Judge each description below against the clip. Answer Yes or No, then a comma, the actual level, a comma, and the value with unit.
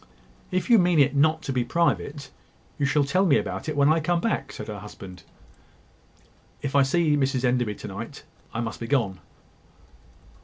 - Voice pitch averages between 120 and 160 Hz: Yes, medium, 140 Hz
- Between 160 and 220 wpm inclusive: Yes, average, 185 wpm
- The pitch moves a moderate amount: Yes, average, 4.5 semitones